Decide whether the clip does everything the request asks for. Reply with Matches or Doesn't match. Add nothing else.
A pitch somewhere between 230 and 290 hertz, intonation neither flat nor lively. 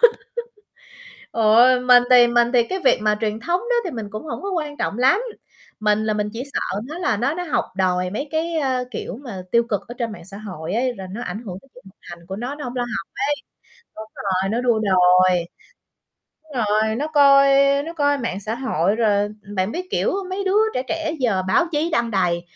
Doesn't match